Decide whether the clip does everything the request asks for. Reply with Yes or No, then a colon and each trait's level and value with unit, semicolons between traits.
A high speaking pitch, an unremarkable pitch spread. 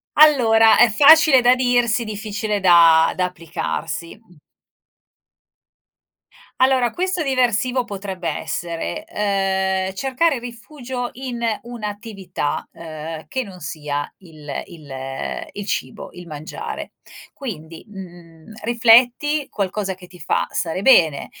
No: high, 205 Hz; wide, 6.4 semitones